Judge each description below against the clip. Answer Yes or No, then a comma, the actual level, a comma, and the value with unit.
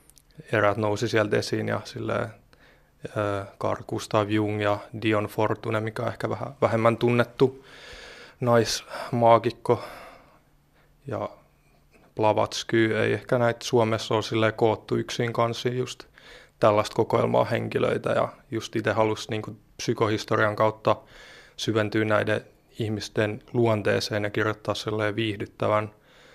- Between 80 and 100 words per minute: No, average, 110 wpm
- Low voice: Yes, low, 110 Hz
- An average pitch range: No, narrow, 1.7 semitones